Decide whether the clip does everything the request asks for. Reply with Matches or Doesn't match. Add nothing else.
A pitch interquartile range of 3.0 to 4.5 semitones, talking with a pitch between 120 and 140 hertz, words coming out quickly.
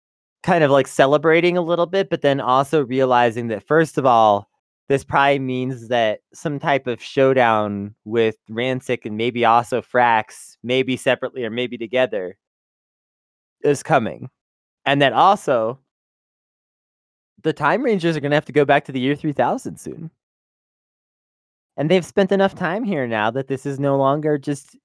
Doesn't match